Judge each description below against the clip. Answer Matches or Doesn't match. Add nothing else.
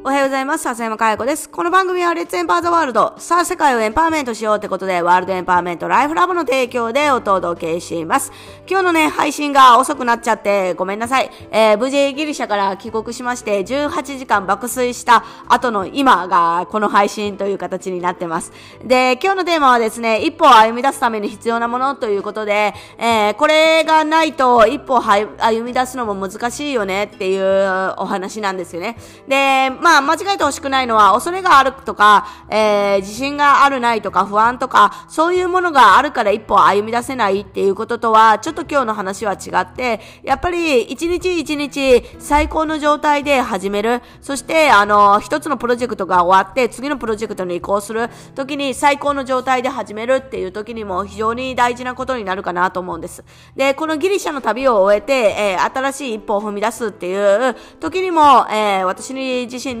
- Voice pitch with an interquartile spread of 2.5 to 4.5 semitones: Doesn't match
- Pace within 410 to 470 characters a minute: Matches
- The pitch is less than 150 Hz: Doesn't match